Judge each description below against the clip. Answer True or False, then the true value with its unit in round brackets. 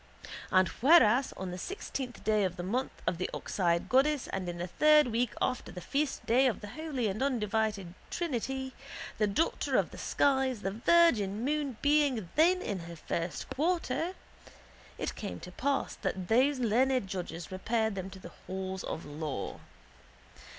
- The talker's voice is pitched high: True (225 Hz)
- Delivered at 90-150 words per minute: False (165 wpm)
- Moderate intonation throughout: False (6.3 semitones)